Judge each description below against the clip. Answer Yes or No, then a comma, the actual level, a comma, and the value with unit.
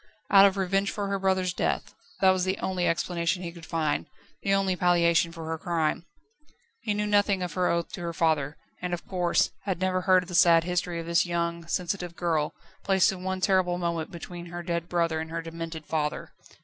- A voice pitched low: No, medium, 175 Hz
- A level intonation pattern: Yes, narrow, 2.0 semitones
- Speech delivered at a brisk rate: Yes, fast, 210 wpm